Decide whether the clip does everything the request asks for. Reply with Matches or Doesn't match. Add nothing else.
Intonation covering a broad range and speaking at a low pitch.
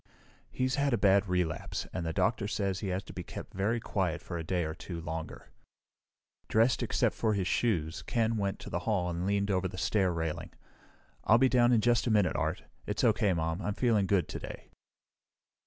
Doesn't match